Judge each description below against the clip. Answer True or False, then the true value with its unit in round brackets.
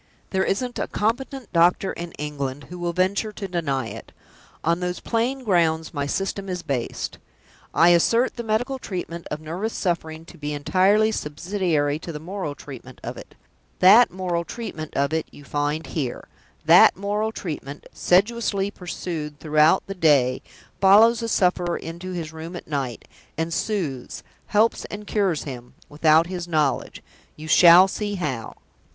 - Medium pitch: True (175 Hz)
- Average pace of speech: True (160 wpm)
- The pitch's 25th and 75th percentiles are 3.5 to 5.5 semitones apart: True (4.8 semitones)